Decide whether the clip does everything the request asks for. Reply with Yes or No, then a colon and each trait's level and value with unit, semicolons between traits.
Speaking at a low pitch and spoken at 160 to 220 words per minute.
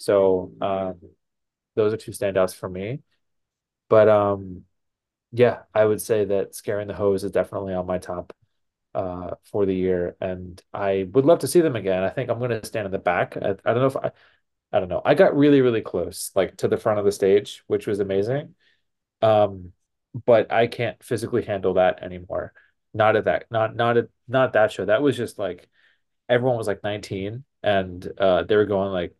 Yes: low, 100 Hz; average, 200 wpm